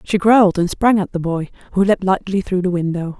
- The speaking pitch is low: No, medium, 185 Hz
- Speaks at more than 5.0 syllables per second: Yes, 5.6 syllables/s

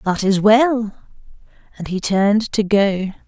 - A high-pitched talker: Yes, high, 205 Hz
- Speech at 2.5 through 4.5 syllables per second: Yes, 4.2 syllables/s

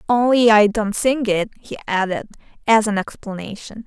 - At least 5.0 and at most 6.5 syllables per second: No, 4.8 syllables/s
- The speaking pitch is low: No, high, 215 Hz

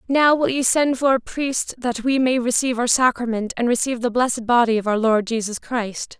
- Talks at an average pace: No, fast, 225 wpm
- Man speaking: No, female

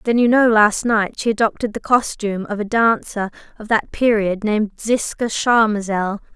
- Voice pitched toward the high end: Yes, high, 215 Hz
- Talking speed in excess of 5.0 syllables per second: No, 4.9 syllables/s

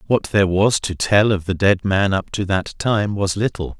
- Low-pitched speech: Yes, low, 100 Hz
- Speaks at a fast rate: Yes, fast, 235 wpm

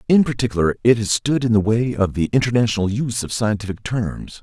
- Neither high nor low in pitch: No, low, 110 Hz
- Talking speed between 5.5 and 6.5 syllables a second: Yes, 6.0 syllables/s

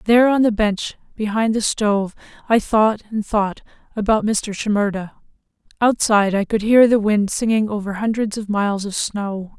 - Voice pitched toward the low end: No, high, 210 Hz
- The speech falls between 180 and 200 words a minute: No, average, 170 wpm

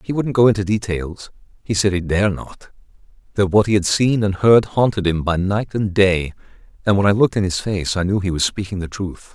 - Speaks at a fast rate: Yes, fast, 240 wpm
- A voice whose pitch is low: Yes, low, 100 Hz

